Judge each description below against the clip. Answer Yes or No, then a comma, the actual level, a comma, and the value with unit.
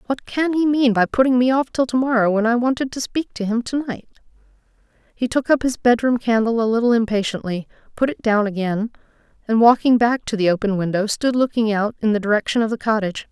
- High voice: Yes, high, 230 Hz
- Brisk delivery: Yes, fast, 220 wpm